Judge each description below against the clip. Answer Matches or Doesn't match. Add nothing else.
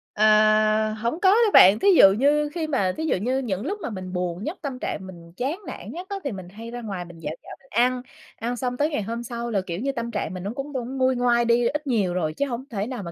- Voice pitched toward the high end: Matches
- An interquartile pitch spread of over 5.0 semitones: Matches